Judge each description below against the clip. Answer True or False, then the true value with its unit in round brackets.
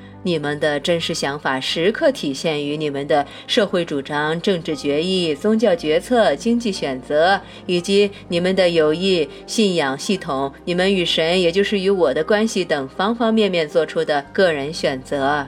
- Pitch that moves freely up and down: False (4.8 semitones)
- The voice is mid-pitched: True (170 Hz)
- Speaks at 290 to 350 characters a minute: False (255 characters per minute)